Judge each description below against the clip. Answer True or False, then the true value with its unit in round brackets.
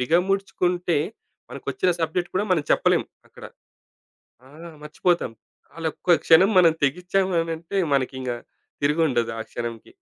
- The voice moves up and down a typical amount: True (4.0 semitones)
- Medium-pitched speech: True (165 Hz)